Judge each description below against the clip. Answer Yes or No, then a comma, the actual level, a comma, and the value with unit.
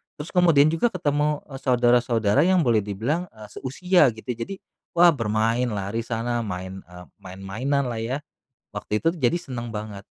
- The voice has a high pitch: No, low, 120 Hz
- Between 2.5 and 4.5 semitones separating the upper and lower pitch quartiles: No, wide, 5.4 semitones